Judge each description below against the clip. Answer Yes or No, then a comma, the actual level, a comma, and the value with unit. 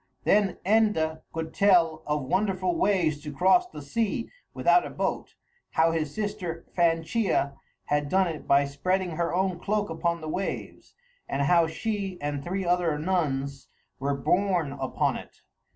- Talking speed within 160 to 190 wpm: No, average, 150 wpm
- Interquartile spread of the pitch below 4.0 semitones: No, average, 4.3 semitones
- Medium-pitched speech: Yes, medium, 170 Hz